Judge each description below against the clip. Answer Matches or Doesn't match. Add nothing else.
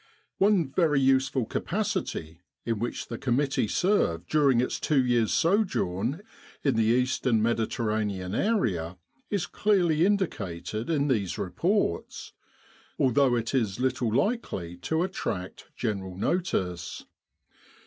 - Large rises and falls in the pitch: Matches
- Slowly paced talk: Matches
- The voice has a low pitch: Matches